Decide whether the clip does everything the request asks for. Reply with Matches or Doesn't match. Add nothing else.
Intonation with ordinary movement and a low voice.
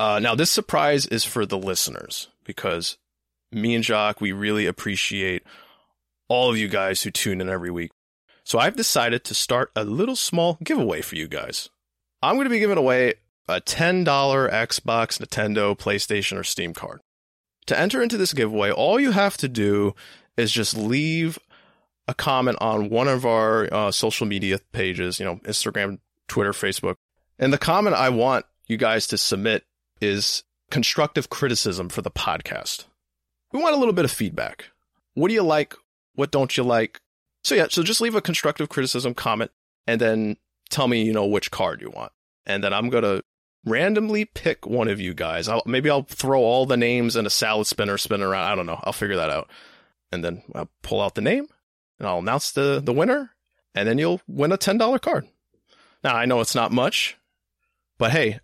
Doesn't match